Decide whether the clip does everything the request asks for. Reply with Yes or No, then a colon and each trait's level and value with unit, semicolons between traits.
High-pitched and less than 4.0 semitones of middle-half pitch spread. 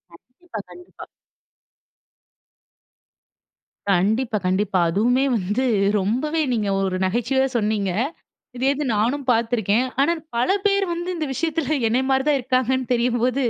No: very high, 250 Hz; average, 4.4 semitones